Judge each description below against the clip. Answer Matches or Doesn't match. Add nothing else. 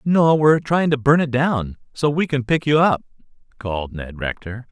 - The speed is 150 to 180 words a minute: Doesn't match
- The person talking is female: Doesn't match